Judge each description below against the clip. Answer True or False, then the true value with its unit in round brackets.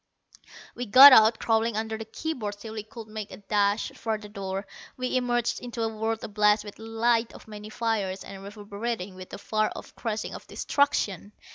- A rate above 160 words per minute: True (200 wpm)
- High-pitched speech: True (220 Hz)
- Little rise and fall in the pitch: True (1.8 semitones)